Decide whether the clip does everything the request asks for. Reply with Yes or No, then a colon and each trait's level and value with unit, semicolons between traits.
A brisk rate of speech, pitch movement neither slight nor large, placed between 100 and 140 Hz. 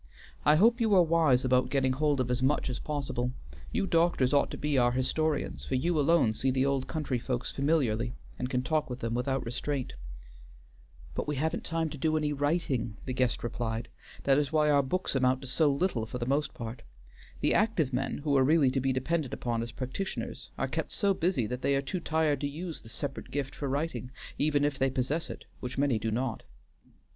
Yes: fast, 215 wpm; average, 3.4 semitones; low, 135 Hz